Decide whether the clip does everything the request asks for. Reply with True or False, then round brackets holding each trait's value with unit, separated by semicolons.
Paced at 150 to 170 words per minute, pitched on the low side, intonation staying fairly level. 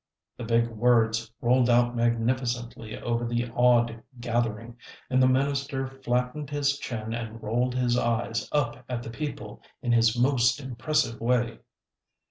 False (140 wpm; 120 Hz; 1.7 semitones)